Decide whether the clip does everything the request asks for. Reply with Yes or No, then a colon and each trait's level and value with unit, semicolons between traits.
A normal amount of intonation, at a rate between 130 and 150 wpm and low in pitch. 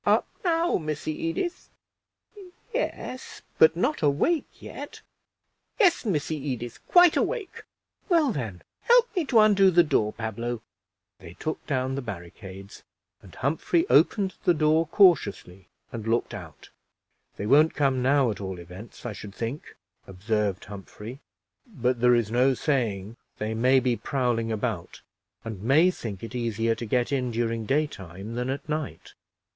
No: wide, 6.2 semitones; average, 145 wpm; low, 125 Hz